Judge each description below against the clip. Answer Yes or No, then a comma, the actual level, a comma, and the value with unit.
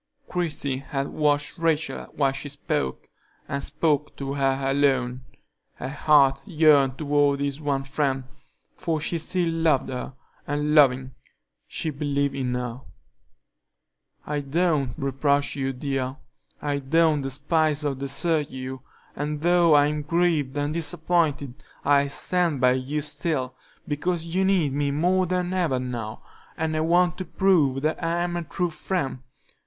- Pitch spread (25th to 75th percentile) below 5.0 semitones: Yes, average, 3.2 semitones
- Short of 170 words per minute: Yes, average, 145 wpm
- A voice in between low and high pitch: Yes, medium, 145 Hz